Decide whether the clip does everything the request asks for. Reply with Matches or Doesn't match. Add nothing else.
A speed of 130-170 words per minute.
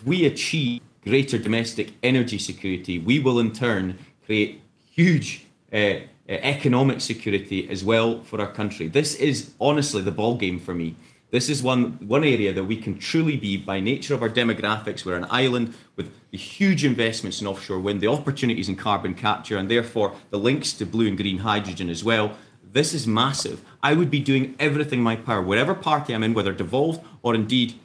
Doesn't match